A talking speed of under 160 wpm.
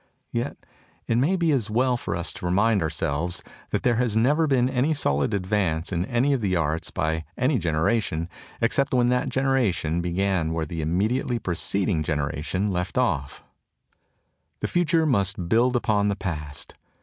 No: average, 165 wpm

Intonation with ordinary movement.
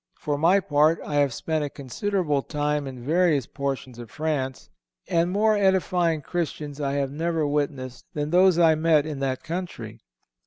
Yes: average, 3.4 semitones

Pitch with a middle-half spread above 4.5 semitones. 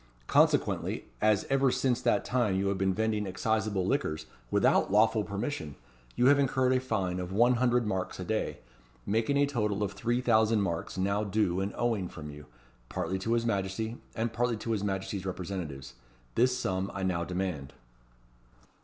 No: average, 3.8 semitones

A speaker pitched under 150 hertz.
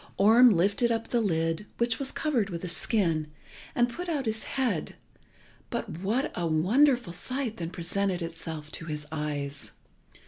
No: high, 200 Hz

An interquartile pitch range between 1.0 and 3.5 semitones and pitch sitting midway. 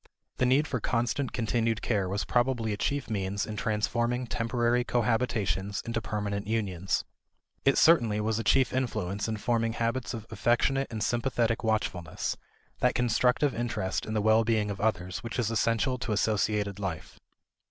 No: narrow, 2.6 semitones; low, 115 Hz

